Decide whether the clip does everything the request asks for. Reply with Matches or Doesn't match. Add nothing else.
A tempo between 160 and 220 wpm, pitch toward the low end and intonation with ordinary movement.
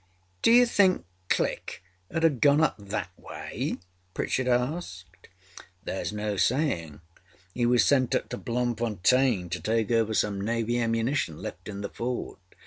Doesn't match